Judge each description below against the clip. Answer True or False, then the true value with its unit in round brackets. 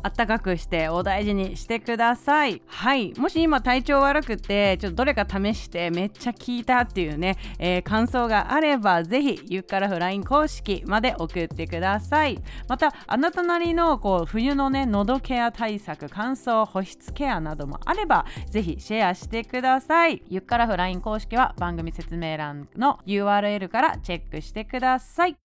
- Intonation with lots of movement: True (6.0 semitones)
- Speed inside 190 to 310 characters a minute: False (355 characters per minute)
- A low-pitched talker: False (220 Hz)